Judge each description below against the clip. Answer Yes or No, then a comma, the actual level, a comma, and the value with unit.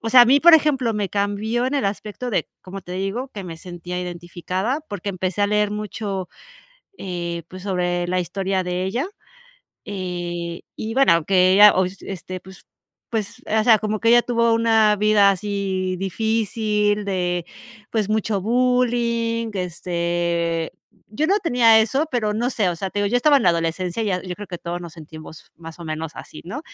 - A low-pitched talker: No, high, 200 Hz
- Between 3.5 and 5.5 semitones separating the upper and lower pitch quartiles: Yes, average, 4.0 semitones